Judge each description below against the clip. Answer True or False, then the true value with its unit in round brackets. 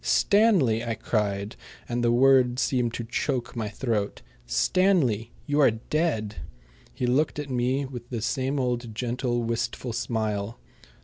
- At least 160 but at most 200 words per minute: False (140 wpm)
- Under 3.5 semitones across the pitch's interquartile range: True (2.9 semitones)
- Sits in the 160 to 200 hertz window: False (120 Hz)